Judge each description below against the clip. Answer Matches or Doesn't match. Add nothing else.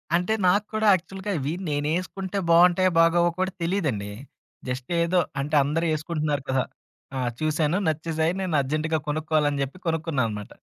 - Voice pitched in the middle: Matches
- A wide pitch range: Doesn't match